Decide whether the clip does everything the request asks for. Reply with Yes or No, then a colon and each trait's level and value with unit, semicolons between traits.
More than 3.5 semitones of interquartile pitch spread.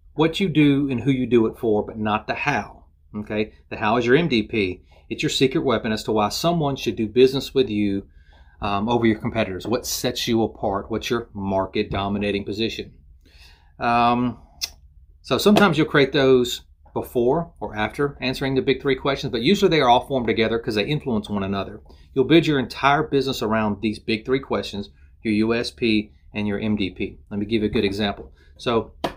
Yes: average, 4.7 semitones